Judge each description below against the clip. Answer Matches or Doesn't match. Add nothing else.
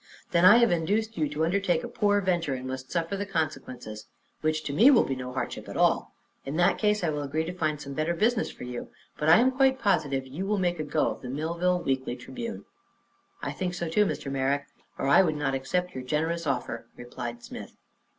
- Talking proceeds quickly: Matches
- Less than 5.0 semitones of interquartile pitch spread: Doesn't match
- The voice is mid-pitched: Matches